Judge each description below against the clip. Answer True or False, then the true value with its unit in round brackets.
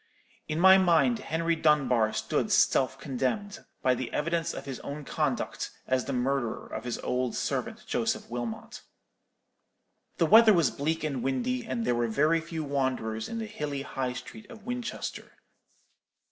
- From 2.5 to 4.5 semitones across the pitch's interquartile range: False (5.4 semitones)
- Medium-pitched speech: True (150 Hz)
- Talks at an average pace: True (160 wpm)